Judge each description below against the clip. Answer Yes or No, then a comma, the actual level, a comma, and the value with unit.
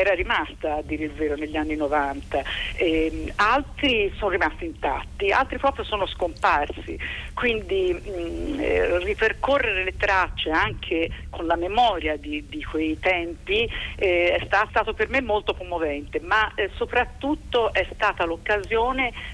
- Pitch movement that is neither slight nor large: No, wide, 8.5 semitones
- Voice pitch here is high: Yes, high, 200 Hz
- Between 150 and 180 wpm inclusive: No, average, 140 wpm